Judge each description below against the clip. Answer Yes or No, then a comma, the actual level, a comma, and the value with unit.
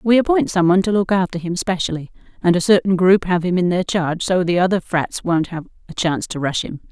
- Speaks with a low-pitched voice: No, medium, 180 Hz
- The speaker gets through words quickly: Yes, fast, 250 wpm